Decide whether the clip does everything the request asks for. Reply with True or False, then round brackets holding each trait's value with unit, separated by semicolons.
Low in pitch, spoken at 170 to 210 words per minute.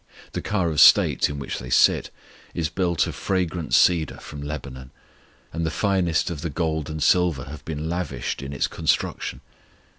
True (80 Hz; 175 wpm)